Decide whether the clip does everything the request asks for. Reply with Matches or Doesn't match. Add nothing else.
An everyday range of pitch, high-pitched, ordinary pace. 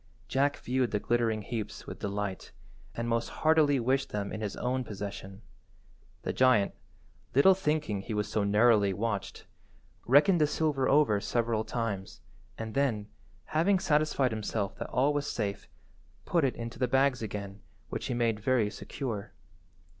Doesn't match